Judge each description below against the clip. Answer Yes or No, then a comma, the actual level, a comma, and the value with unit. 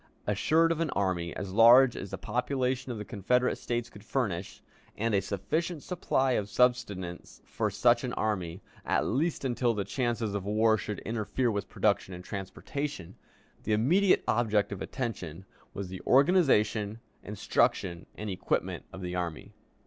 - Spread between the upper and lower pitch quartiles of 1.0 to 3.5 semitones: No, average, 4.5 semitones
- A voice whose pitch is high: No, low, 110 Hz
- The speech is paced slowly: No, average, 155 wpm